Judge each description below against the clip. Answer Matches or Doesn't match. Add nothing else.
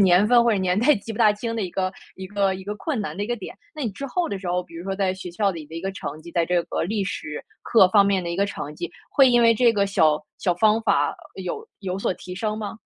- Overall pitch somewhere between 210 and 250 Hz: Doesn't match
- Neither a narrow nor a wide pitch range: Matches